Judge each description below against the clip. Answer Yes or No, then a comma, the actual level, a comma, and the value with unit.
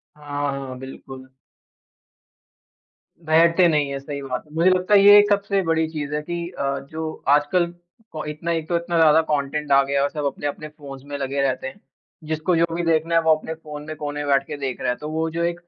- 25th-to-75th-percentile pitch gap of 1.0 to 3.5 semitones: Yes, average, 2.8 semitones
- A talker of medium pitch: Yes, medium, 150 Hz